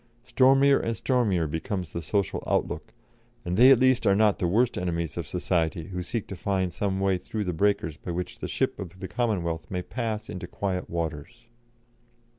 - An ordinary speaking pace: Yes, average, 190 wpm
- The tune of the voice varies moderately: Yes, average, 4.5 semitones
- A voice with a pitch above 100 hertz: No, very low, 95 Hz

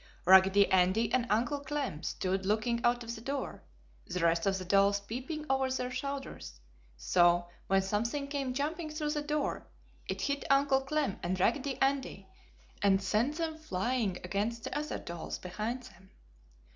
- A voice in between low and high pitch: No, high, 235 Hz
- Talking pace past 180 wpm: No, average, 160 wpm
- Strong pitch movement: Yes, wide, 6.4 semitones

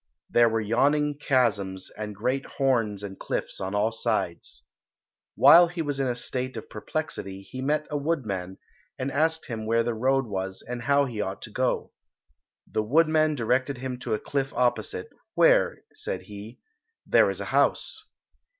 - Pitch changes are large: No, average, 4.8 semitones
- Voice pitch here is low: Yes, low, 125 Hz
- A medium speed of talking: Yes, average, 170 wpm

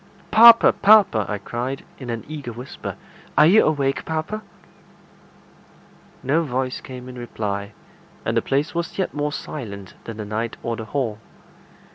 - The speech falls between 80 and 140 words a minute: No, average, 150 wpm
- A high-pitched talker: No, low, 130 Hz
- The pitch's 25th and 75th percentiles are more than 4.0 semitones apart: Yes, wide, 5.4 semitones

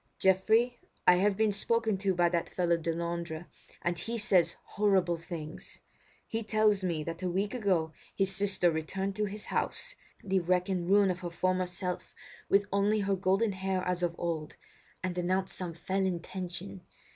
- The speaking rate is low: No, average, 175 wpm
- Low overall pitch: No, medium, 185 Hz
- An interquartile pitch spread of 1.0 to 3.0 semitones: Yes, narrow, 2.4 semitones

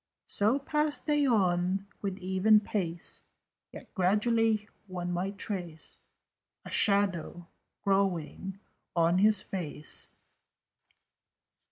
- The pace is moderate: No, slow, 90 wpm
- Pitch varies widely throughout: No, average, 3.2 semitones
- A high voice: Yes, high, 195 Hz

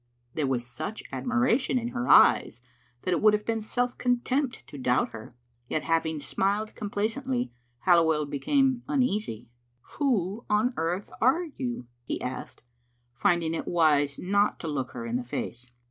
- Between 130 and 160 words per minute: Yes, average, 155 wpm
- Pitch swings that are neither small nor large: No, wide, 9.0 semitones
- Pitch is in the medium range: No, high, 200 Hz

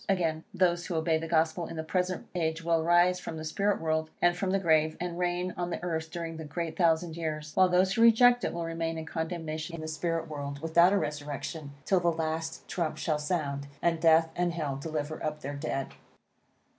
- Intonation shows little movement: Yes, narrow, 1.9 semitones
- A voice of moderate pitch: Yes, medium, 165 Hz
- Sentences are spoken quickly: Yes, fast, 215 wpm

